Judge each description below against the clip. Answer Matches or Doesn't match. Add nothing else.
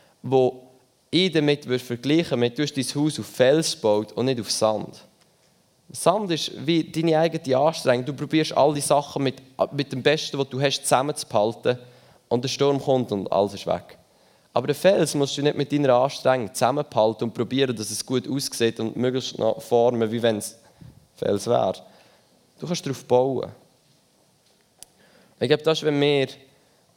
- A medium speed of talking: Matches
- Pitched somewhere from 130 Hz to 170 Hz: Matches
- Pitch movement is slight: Doesn't match